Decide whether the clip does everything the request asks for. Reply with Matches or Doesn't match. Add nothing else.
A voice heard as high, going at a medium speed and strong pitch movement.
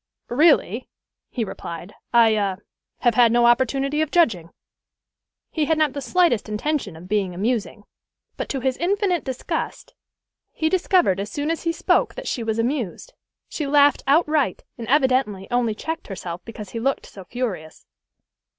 Matches